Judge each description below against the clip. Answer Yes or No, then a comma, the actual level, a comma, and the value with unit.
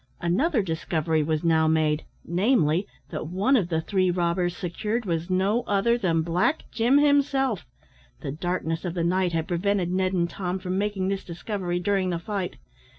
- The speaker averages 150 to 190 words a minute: Yes, average, 170 wpm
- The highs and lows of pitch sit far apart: No, average, 3.3 semitones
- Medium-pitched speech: Yes, medium, 180 Hz